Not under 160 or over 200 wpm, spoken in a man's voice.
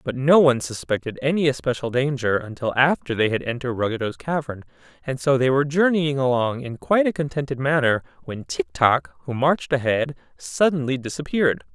Yes: average, 170 wpm; male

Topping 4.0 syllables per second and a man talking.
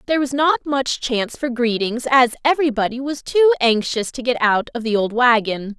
No: 5.4 syllables/s; female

